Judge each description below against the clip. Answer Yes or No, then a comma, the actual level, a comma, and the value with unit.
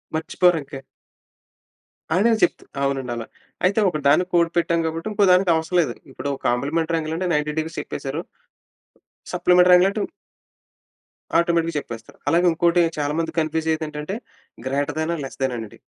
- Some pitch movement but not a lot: Yes, average, 3.3 semitones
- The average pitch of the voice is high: No, medium, 160 Hz